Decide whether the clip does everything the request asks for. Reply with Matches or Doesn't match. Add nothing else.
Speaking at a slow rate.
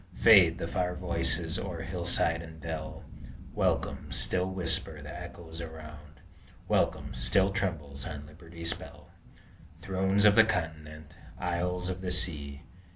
Matches